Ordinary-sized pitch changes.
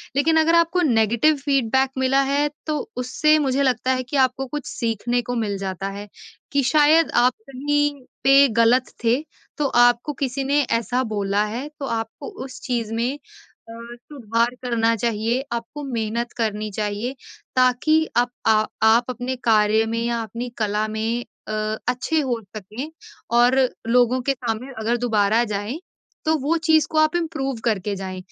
Yes: average, 3.7 semitones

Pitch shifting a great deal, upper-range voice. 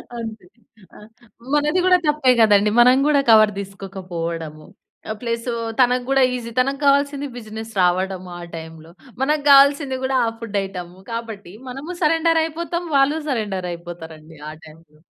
Yes: wide, 7.3 semitones; high, 230 Hz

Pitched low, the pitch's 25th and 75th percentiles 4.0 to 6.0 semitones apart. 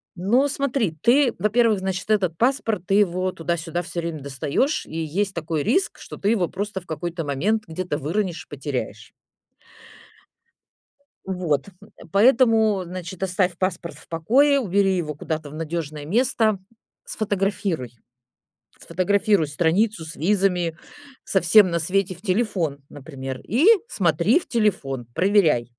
No: medium, 185 Hz; average, 4.6 semitones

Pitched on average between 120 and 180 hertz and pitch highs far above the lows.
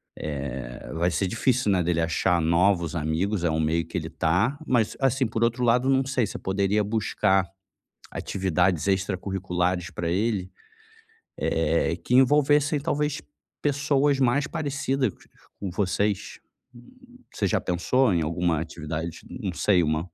No: very low, 95 Hz; wide, 6.7 semitones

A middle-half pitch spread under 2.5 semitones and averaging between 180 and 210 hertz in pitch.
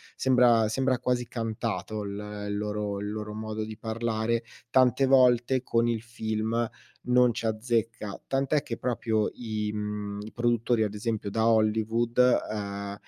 No: narrow, 2.1 semitones; low, 110 Hz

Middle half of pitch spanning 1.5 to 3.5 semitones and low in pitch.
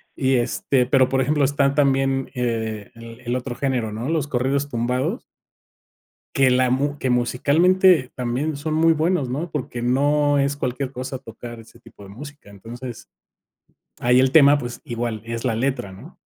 Yes: average, 2.9 semitones; low, 130 Hz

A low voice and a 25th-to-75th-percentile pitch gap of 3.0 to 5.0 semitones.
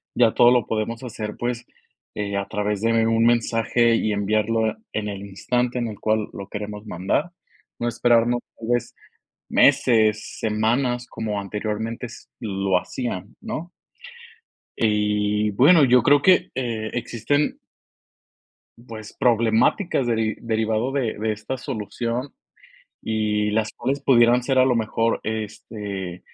No: low, 110 Hz; narrow, 2.4 semitones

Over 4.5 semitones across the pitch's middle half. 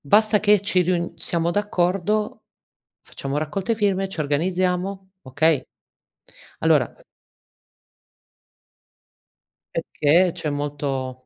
Yes: average, 4.9 semitones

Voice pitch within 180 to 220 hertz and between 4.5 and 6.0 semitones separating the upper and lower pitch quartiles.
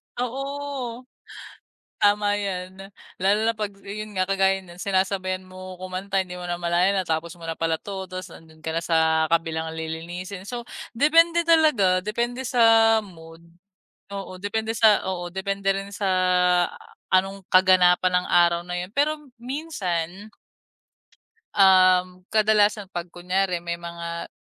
No: high, 190 Hz; average, 3.2 semitones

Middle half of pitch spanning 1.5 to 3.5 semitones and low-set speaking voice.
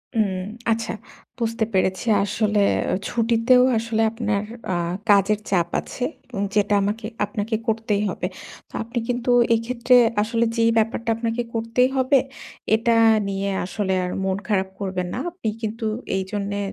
No: narrow, 2.5 semitones; high, 220 Hz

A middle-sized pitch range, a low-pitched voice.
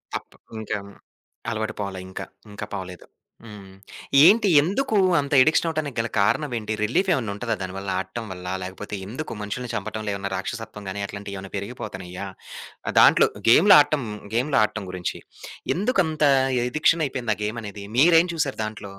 No: wide, 6.6 semitones; low, 110 Hz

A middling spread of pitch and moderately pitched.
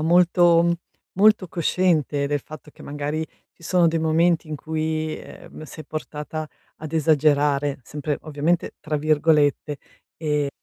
No: narrow, 2.1 semitones; medium, 155 Hz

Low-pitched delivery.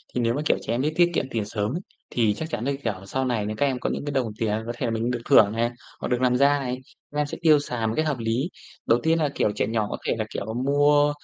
Yes: low, 125 Hz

